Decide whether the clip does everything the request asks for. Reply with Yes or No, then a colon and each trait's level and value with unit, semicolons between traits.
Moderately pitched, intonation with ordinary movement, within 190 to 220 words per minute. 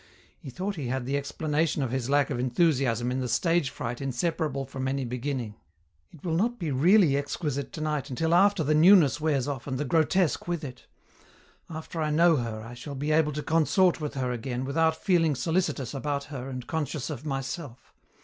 Yes: medium, 145 Hz; average, 3.7 semitones; average, 195 wpm